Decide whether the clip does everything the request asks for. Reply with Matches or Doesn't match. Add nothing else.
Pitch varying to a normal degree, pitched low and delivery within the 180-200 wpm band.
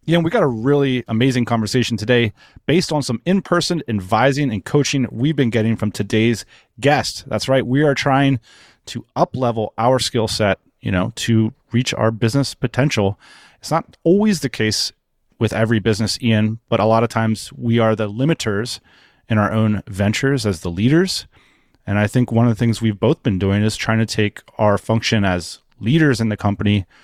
Matches